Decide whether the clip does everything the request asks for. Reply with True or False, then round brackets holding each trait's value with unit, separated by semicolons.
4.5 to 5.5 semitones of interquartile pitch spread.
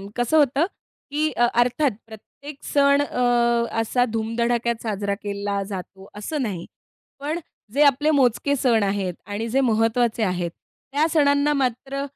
True (5.2 semitones)